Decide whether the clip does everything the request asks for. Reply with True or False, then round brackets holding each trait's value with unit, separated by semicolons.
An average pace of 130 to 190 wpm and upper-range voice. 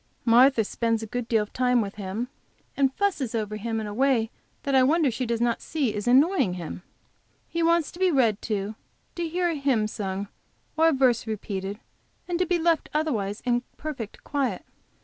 False (200 wpm; 245 Hz)